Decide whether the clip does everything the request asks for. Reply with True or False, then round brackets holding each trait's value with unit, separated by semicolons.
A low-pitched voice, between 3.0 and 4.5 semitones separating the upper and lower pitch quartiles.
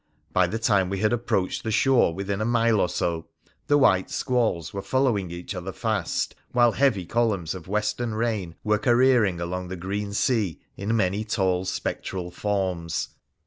True (100 Hz; 3.9 semitones)